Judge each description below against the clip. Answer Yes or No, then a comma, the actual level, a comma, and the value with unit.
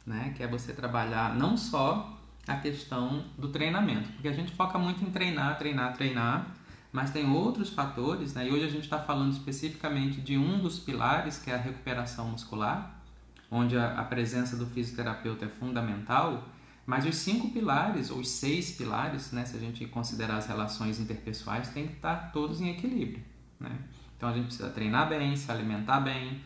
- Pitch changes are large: No, average, 4.2 semitones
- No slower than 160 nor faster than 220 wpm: Yes, fast, 185 wpm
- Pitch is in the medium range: No, low, 130 Hz